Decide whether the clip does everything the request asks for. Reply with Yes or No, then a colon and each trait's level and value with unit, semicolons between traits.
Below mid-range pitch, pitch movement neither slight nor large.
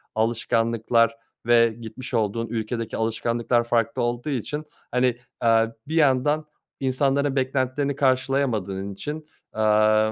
Yes: low, 120 Hz; average, 3.0 semitones